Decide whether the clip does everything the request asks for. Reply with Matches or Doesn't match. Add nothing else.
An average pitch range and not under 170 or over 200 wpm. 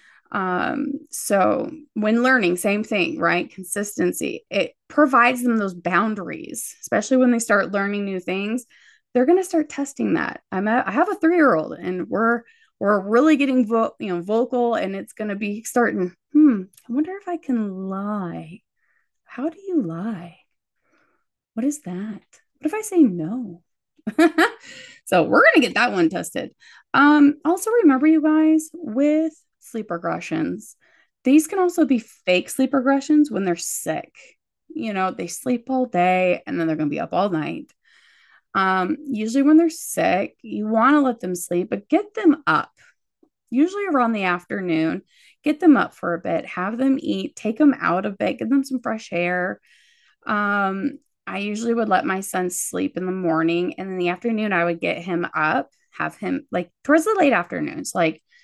Doesn't match